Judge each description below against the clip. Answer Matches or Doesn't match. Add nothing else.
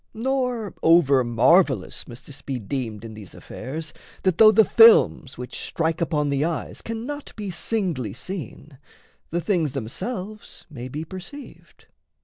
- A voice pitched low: Doesn't match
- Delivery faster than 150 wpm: Doesn't match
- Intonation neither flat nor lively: Doesn't match